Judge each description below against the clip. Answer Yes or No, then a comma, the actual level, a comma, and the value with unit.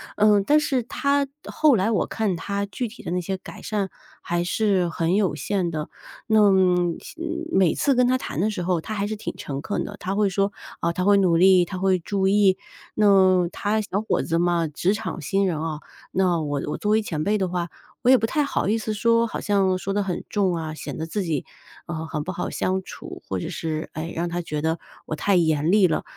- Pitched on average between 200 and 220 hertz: No, high, 190 Hz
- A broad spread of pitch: No, average, 3.5 semitones